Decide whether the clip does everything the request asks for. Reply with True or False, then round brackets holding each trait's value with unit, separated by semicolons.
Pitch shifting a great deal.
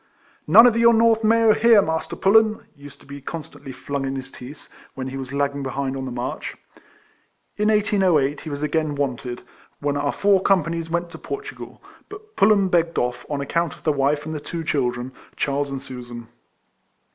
True (6.2 semitones)